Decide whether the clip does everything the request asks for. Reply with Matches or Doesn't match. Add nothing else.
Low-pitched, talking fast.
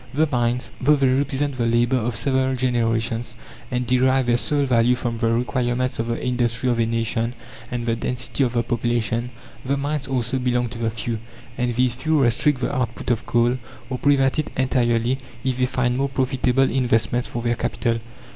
Doesn't match